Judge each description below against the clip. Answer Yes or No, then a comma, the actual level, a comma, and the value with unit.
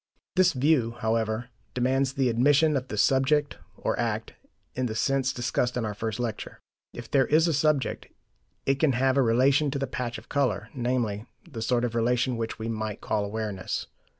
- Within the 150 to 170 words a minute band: No, average, 185 wpm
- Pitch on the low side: Yes, low, 125 Hz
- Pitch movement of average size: Yes, average, 3.3 semitones